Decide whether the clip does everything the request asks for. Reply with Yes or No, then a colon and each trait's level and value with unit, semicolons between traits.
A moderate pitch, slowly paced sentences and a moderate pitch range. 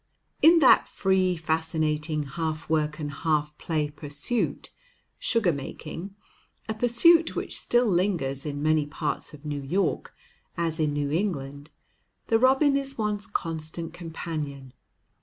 Yes: medium, 160 Hz; slow, 130 wpm; average, 4.9 semitones